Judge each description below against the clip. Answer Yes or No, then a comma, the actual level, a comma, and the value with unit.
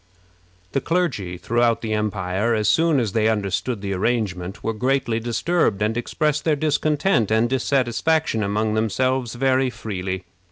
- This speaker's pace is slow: No, average, 145 wpm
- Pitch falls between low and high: No, low, 115 Hz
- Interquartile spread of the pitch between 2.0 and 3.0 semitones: No, average, 4.0 semitones